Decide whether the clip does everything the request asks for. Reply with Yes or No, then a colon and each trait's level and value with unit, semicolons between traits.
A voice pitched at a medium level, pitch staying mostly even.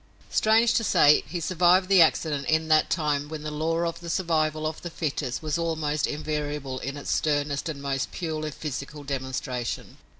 Yes: medium, 155 Hz; narrow, 2.3 semitones